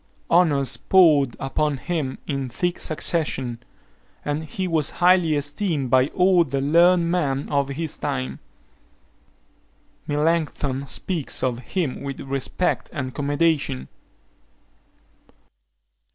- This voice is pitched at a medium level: Yes, medium, 145 Hz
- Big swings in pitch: No, average, 3.9 semitones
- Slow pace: Yes, slow, 105 wpm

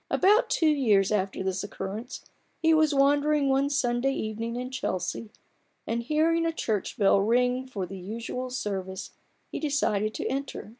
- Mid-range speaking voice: No, high, 245 Hz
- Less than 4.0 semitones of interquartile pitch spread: No, wide, 5.6 semitones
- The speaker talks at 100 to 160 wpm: Yes, average, 155 wpm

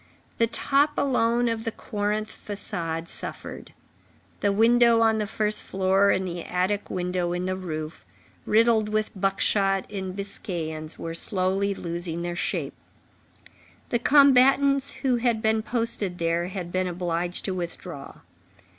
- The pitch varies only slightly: No, average, 4.3 semitones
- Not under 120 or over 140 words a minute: Yes, slow, 135 wpm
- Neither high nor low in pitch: No, high, 195 Hz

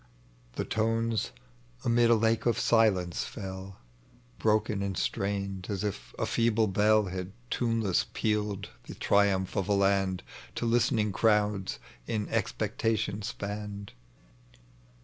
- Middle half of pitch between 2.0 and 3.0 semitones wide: Yes, narrow, 2.4 semitones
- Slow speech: Yes, slow, 120 wpm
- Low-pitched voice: Yes, low, 105 Hz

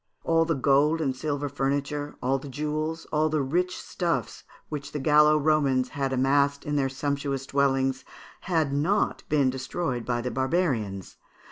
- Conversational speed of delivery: Yes, average, 160 wpm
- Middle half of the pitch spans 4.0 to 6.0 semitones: No, narrow, 2.4 semitones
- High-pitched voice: No, medium, 140 Hz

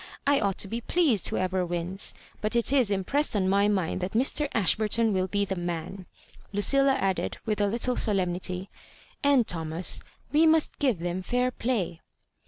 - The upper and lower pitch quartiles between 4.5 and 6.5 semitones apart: Yes, average, 5.1 semitones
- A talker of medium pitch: No, high, 205 Hz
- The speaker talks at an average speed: Yes, average, 170 wpm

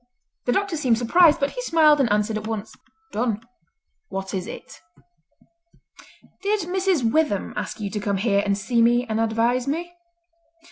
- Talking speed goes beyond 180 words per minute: No, average, 160 wpm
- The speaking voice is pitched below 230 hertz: No, high, 240 Hz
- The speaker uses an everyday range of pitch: No, wide, 6.9 semitones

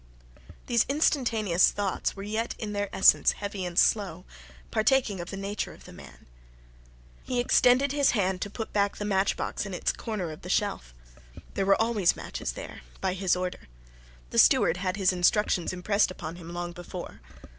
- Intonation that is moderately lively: Yes, average, 3.2 semitones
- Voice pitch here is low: No, high, 195 Hz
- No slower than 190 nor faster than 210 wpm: No, average, 175 wpm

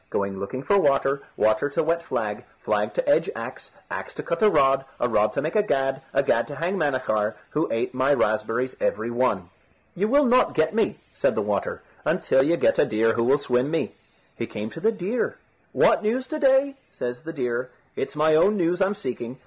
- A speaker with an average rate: No, fast, 215 wpm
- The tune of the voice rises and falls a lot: Yes, wide, 7.8 semitones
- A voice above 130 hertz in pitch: Yes, medium, 140 Hz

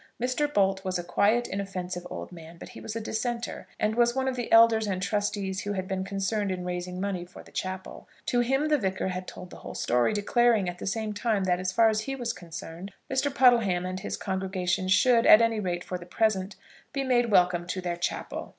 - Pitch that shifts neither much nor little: Yes, average, 3.9 semitones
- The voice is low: No, high, 195 Hz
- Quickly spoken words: Yes, fast, 225 wpm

